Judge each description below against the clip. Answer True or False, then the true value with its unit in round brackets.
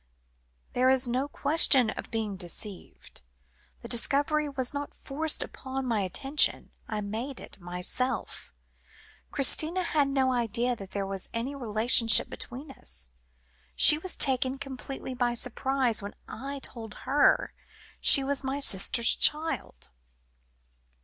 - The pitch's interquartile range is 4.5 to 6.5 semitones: False (3.8 semitones)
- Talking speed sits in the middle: False (130 wpm)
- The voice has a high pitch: True (255 Hz)